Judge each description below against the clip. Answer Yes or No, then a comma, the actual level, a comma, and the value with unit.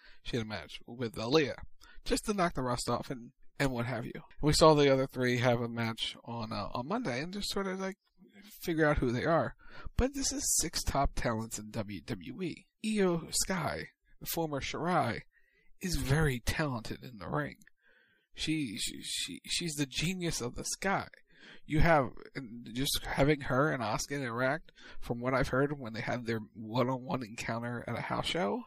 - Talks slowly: No, average, 195 wpm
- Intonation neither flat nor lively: No, wide, 5.7 semitones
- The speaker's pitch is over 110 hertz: Yes, low, 135 Hz